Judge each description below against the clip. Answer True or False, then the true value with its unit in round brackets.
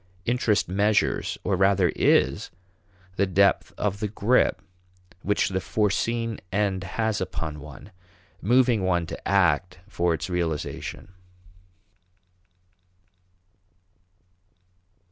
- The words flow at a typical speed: False (95 wpm)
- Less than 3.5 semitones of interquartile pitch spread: True (2.9 semitones)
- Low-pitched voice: True (100 Hz)